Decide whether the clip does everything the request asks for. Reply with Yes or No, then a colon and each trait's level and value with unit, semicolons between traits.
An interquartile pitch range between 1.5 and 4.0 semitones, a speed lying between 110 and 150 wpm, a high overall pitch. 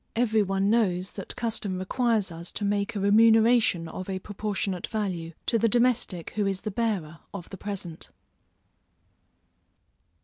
Yes: average, 3.2 semitones; average, 145 wpm; high, 200 Hz